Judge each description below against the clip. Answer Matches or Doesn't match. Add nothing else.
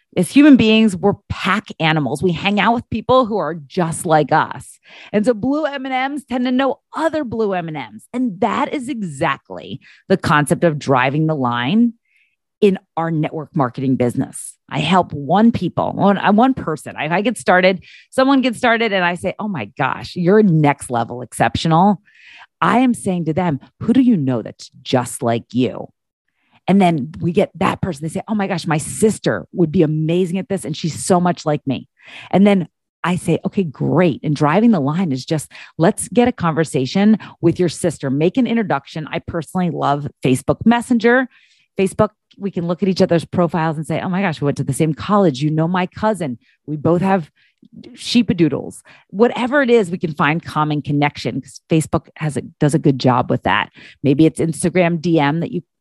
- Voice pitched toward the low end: Doesn't match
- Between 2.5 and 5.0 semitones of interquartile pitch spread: Doesn't match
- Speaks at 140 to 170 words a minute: Doesn't match